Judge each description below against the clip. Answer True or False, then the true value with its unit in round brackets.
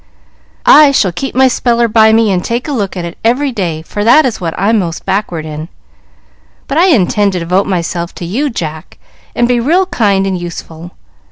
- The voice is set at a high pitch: True (205 Hz)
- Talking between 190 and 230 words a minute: True (200 wpm)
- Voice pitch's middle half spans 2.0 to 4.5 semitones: False (5.6 semitones)